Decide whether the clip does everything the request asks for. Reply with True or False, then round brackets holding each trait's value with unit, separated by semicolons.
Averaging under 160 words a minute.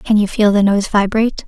False (245 wpm)